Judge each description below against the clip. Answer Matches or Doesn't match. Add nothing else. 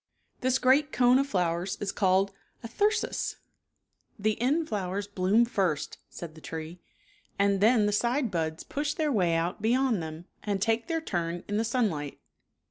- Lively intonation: Matches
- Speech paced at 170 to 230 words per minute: Matches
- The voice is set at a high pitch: Matches